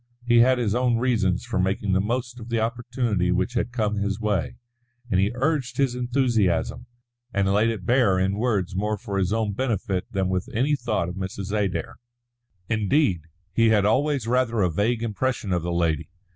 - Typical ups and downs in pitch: Yes, average, 4.2 semitones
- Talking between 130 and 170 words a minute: No, average, 185 wpm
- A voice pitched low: Yes, low, 110 Hz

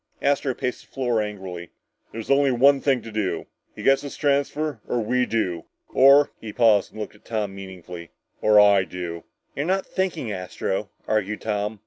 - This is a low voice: Yes, low, 110 Hz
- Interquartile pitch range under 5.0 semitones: No, wide, 5.6 semitones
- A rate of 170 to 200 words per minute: Yes, average, 180 wpm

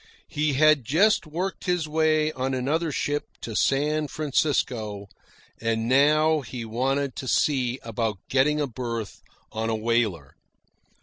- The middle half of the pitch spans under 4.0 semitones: No, average, 4.8 semitones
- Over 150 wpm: No, slow, 135 wpm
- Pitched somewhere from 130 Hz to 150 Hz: Yes, low, 135 Hz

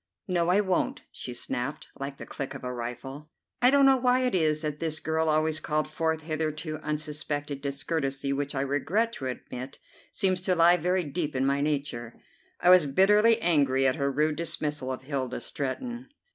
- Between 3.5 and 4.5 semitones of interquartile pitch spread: Yes, average, 4.1 semitones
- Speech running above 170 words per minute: Yes, average, 185 wpm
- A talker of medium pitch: Yes, medium, 150 Hz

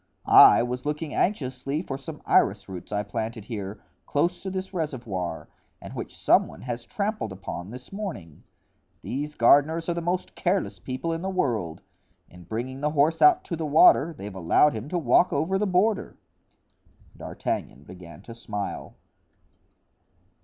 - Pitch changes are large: Yes, wide, 8.1 semitones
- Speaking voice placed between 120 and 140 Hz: Yes, low, 135 Hz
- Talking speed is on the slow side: No, average, 160 wpm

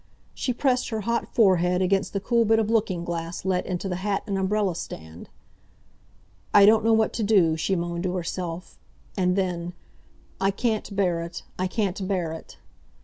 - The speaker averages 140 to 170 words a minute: No, average, 180 wpm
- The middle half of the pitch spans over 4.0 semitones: No, average, 3.2 semitones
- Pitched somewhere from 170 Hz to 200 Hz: Yes, high, 190 Hz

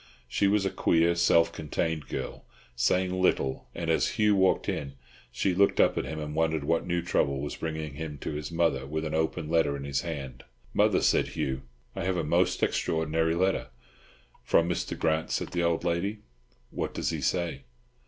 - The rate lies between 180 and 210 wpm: Yes, average, 195 wpm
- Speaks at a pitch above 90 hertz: No, very low, 80 Hz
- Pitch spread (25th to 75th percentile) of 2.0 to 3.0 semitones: Yes, narrow, 2.6 semitones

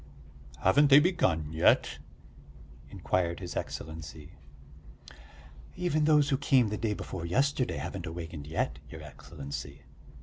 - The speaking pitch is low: Yes, very low, 85 Hz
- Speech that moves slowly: Yes, slow, 115 wpm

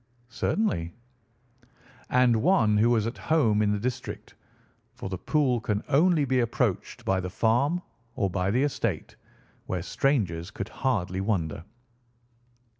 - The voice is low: Yes, low, 110 Hz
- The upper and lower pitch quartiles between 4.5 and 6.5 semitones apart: Yes, wide, 5.5 semitones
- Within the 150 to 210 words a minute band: No, slow, 135 wpm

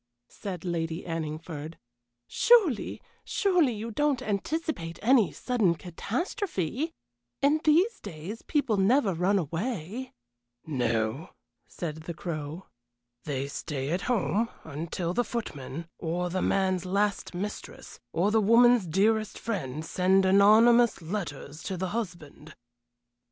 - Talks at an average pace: No, slow, 120 wpm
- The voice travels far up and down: Yes, wide, 6.2 semitones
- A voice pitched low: No, high, 190 Hz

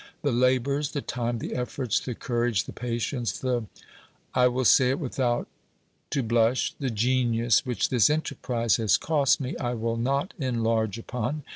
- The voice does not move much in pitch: Yes, narrow, 2.1 semitones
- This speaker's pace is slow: No, average, 160 wpm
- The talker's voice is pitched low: Yes, low, 125 Hz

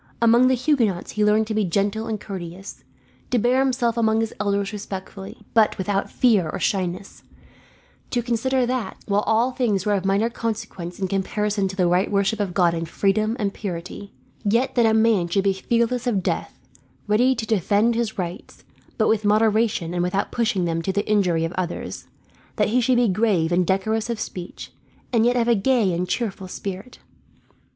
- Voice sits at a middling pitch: No, high, 210 Hz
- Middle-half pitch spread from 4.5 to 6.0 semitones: No, average, 3.3 semitones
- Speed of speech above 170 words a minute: Yes, average, 190 wpm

